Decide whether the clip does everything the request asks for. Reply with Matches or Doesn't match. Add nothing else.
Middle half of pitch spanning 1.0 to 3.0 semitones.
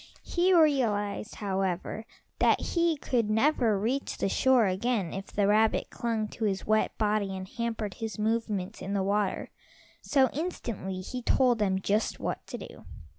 Doesn't match